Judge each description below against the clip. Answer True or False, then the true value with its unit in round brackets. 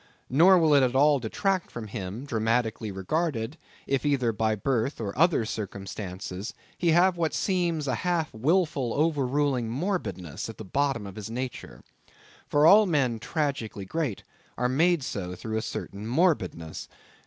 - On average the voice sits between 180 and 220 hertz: False (130 Hz)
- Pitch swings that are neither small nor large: False (6.4 semitones)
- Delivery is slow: False (155 wpm)